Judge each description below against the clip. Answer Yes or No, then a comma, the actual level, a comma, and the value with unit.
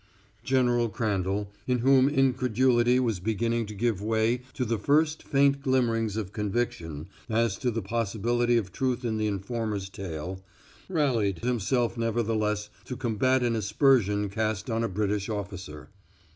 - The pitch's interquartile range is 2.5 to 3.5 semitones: Yes, average, 3.2 semitones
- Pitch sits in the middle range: No, low, 115 Hz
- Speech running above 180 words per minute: No, average, 145 wpm